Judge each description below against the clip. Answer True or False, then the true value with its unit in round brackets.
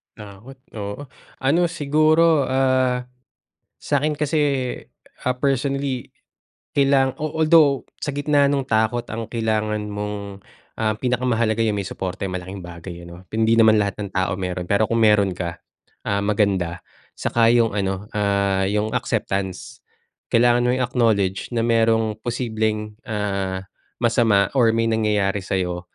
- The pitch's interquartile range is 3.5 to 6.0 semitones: True (4.2 semitones)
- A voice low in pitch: True (110 Hz)